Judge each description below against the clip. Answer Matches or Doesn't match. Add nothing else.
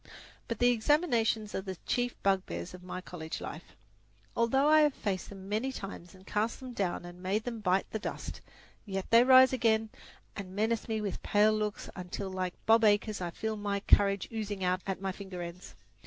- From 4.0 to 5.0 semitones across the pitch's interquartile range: Doesn't match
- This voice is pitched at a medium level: Doesn't match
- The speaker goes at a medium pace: Matches